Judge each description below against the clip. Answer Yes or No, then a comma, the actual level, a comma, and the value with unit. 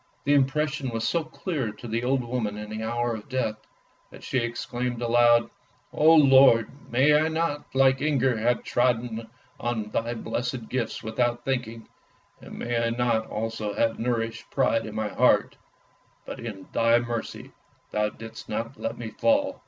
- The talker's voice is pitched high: No, low, 120 Hz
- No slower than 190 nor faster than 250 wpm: No, average, 170 wpm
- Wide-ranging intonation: No, narrow, 2.6 semitones